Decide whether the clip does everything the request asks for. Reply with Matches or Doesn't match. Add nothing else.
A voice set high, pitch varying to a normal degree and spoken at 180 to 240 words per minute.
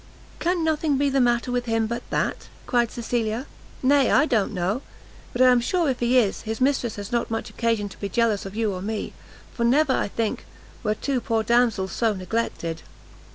Matches